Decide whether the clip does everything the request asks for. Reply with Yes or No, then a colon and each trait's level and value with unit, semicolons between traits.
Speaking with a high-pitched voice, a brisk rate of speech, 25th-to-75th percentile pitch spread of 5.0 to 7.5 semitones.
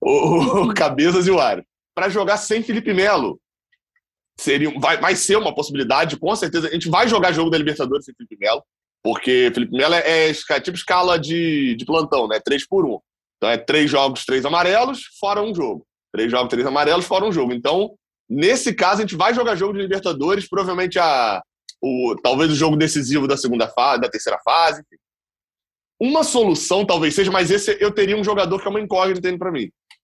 No: medium, 180 Hz; fast, 195 wpm; average, 5.3 semitones